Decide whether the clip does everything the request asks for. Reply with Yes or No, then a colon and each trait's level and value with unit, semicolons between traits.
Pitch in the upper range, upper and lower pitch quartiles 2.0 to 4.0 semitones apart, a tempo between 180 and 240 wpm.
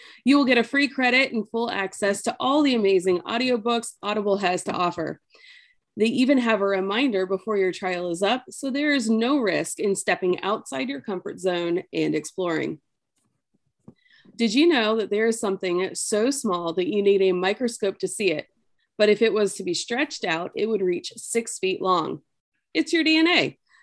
No: high, 215 Hz; average, 4.9 semitones; average, 190 wpm